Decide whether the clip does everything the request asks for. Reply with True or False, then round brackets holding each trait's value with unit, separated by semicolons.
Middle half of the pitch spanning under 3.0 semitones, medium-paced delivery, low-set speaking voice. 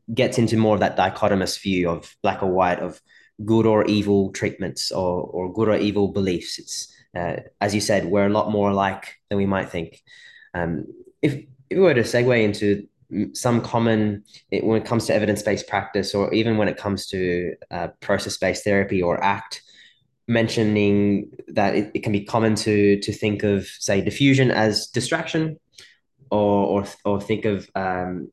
True (2.4 semitones; 180 wpm; 105 Hz)